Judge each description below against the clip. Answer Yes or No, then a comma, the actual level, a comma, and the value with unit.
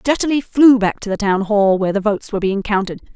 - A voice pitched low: No, high, 210 Hz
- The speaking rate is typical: No, fast, 245 wpm